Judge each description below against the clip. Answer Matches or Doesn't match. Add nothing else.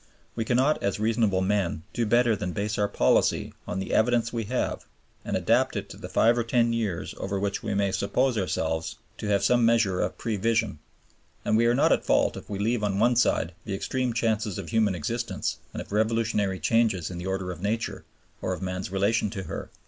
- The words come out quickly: Matches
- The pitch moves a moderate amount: Matches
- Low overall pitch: Matches